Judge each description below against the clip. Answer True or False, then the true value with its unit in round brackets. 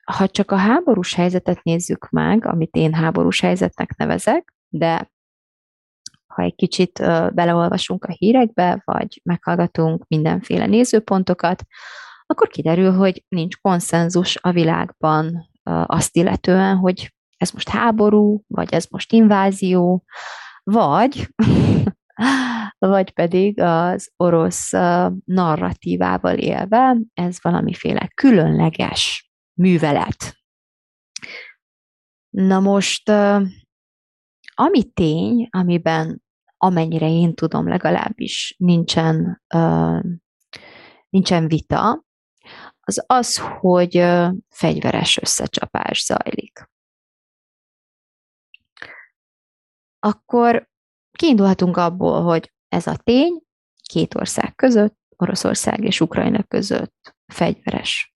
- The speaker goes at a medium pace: False (85 wpm)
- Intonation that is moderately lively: True (4.0 semitones)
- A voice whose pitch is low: False (180 Hz)